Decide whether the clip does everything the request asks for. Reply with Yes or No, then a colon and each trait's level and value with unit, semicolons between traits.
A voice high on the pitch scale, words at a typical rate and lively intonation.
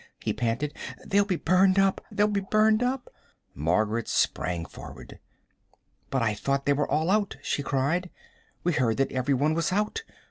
No: medium, 155 Hz; average, 170 wpm; wide, 7.2 semitones